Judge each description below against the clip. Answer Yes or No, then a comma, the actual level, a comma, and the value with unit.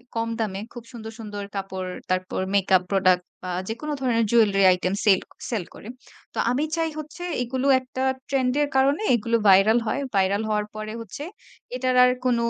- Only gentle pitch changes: No, average, 4.6 semitones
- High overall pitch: Yes, high, 225 Hz